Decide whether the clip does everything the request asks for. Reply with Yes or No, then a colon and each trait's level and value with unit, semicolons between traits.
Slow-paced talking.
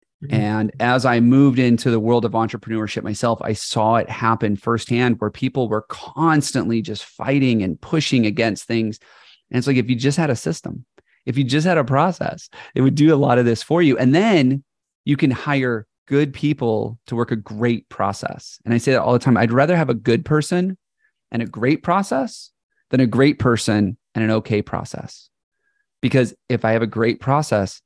No: average, 200 wpm